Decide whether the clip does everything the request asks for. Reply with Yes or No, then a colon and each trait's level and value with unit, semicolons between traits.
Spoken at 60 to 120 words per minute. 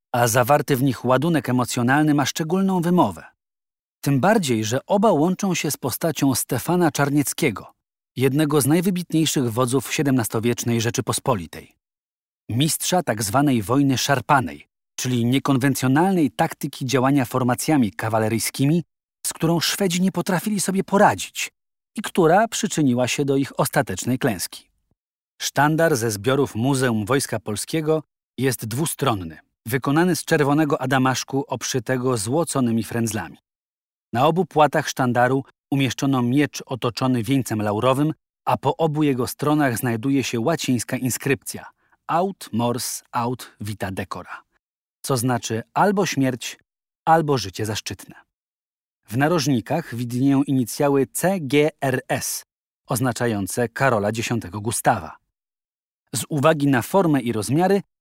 Yes: average, 115 wpm